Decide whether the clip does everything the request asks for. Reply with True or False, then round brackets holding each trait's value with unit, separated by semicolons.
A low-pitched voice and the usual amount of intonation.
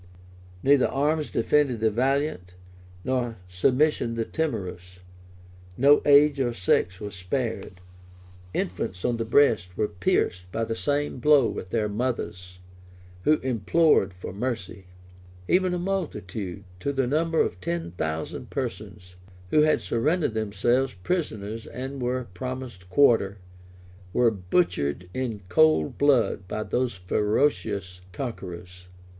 False (115 Hz; 6.9 semitones)